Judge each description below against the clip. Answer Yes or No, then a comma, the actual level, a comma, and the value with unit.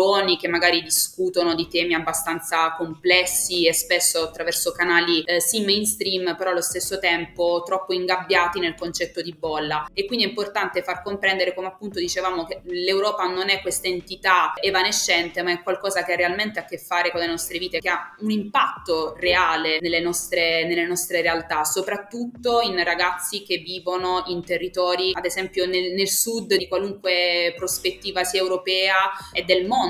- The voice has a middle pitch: Yes, medium, 180 Hz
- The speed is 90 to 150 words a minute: No, average, 165 wpm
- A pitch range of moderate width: No, narrow, 1.6 semitones